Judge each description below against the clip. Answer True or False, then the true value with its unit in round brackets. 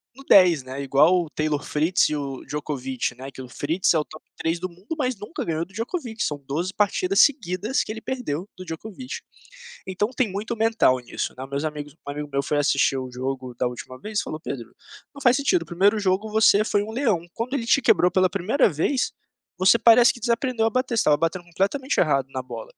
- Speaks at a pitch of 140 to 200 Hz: True (185 Hz)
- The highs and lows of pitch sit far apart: True (7.5 semitones)